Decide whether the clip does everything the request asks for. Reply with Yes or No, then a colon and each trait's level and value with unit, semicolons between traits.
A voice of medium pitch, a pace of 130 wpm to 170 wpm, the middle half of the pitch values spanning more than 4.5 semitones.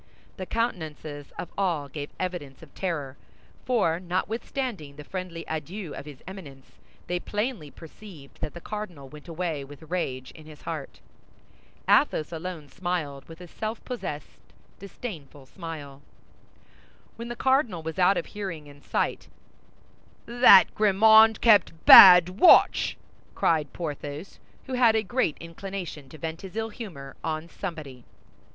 Yes: medium, 170 Hz; average, 140 wpm; average, 5.1 semitones